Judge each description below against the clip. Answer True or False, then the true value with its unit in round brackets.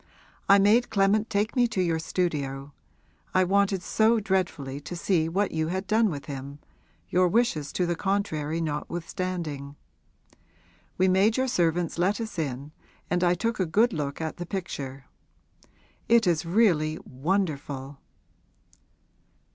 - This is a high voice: False (175 Hz)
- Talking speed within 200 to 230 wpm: False (140 wpm)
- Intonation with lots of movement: False (4.8 semitones)